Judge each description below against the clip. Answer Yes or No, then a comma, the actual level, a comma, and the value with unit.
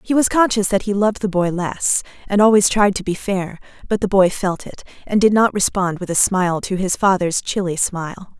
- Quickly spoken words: Yes, fast, 230 wpm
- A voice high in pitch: Yes, high, 195 Hz